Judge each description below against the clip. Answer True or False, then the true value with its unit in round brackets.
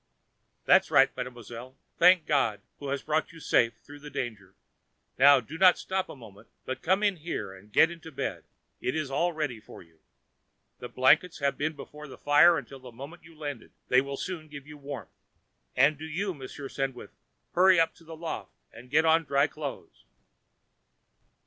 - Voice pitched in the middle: True (145 Hz)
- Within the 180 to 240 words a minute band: True (185 wpm)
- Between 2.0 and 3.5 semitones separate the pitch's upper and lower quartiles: False (4.0 semitones)